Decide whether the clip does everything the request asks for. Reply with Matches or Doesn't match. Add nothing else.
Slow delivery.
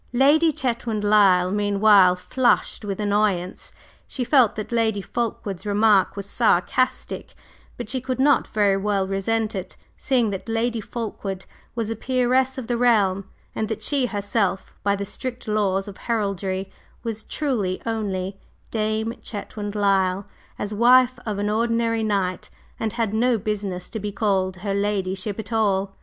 Doesn't match